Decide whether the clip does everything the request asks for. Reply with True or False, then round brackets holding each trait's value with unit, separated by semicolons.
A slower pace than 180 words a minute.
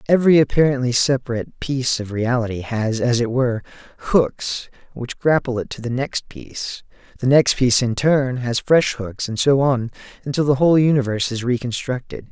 True (170 wpm)